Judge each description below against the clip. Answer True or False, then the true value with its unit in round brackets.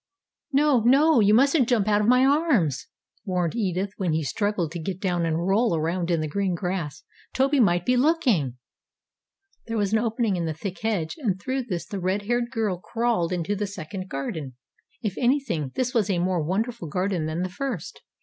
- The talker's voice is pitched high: True (195 Hz)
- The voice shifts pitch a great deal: True (5.7 semitones)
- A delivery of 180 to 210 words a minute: True (195 wpm)